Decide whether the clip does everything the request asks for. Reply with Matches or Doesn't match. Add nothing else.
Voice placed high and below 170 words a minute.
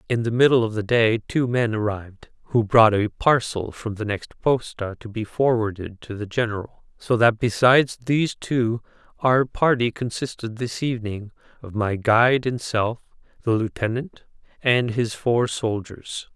Doesn't match